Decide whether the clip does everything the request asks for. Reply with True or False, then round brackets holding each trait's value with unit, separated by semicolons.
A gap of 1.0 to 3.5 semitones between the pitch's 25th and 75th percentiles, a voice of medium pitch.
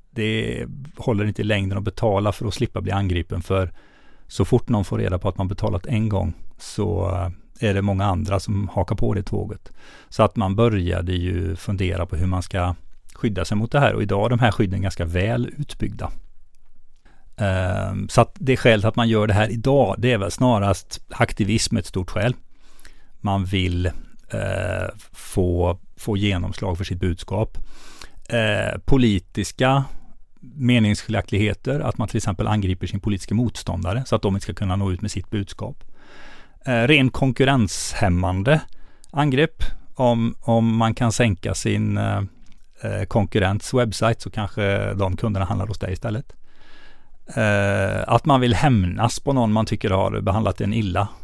False (3.2 semitones; 105 Hz)